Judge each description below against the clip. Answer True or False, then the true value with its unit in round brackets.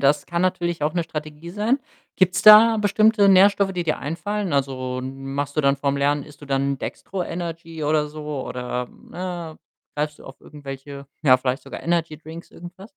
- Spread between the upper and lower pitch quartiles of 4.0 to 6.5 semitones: True (4.4 semitones)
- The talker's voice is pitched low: False (155 Hz)